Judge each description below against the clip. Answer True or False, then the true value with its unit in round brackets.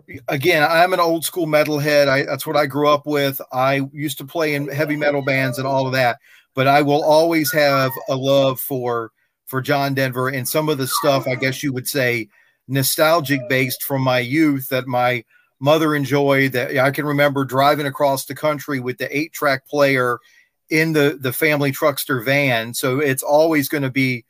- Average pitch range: False (2.0 semitones)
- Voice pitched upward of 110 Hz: True (140 Hz)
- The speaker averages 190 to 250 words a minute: True (200 wpm)